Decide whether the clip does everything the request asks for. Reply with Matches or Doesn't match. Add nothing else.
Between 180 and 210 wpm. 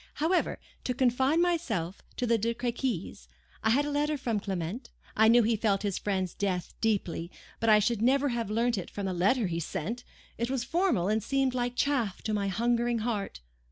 Matches